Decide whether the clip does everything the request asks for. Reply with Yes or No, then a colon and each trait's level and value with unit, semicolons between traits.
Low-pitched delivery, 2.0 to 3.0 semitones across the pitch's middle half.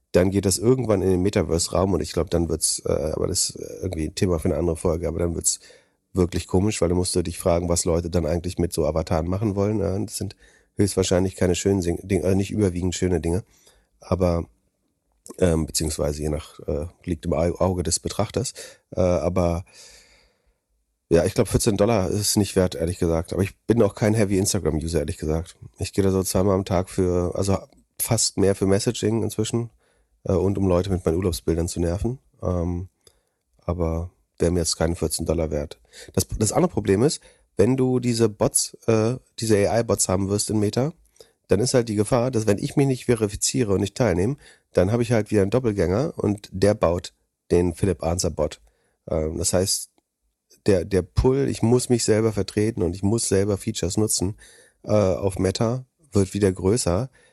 No: very low, 95 Hz; average, 3.7 semitones